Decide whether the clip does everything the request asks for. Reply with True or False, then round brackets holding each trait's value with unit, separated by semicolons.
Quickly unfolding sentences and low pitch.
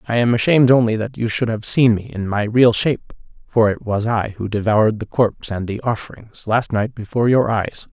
True (220 wpm; 110 Hz)